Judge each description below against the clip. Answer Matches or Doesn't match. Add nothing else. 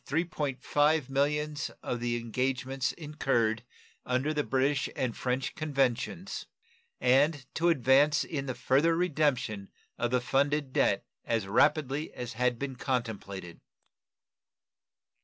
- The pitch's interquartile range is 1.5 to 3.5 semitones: Matches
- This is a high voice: Doesn't match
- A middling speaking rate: Doesn't match